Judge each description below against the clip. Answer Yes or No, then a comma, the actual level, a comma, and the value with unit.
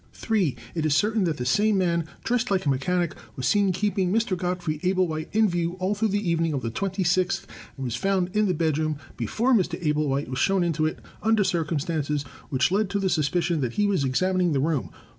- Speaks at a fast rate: Yes, fast, 215 wpm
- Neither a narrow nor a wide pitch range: Yes, average, 4.2 semitones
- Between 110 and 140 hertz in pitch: No, medium, 175 Hz